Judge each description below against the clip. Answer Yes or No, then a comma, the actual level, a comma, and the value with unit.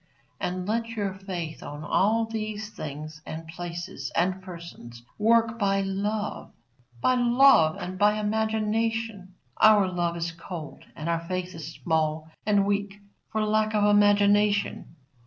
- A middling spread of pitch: Yes, average, 4.0 semitones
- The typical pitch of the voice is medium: No, high, 195 Hz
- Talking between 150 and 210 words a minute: No, average, 140 wpm